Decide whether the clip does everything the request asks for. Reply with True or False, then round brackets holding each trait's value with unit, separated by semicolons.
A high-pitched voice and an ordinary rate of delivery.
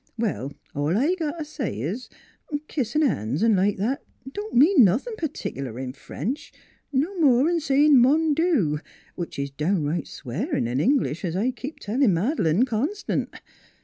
True (235 Hz; 160 wpm)